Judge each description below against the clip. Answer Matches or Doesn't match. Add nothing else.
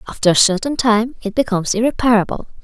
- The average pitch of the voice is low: Doesn't match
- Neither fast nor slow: Matches